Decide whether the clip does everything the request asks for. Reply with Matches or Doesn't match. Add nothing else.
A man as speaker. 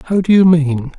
Matches